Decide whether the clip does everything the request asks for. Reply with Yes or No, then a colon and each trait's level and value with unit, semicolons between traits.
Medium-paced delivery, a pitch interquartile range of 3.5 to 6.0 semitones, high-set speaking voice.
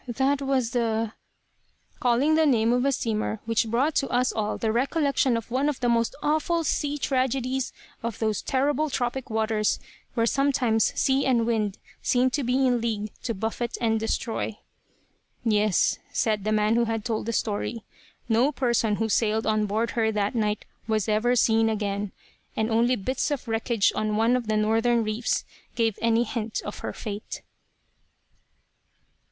No: average, 170 wpm; average, 2.7 semitones; high, 230 Hz